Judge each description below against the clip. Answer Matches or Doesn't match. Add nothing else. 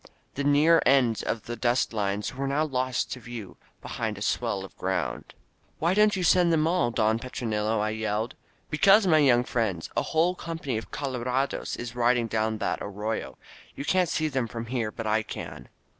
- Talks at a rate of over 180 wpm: Matches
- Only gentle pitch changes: Doesn't match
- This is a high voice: Doesn't match